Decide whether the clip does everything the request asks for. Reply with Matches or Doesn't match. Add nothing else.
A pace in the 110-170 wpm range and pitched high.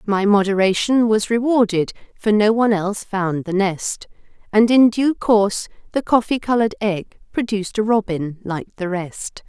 Matches